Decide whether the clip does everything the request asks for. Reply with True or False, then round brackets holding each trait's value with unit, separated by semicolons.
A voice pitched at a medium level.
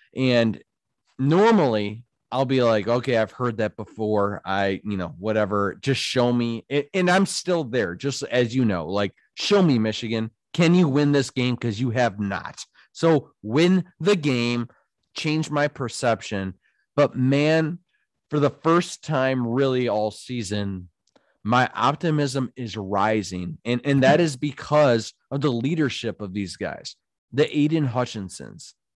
False (125 Hz)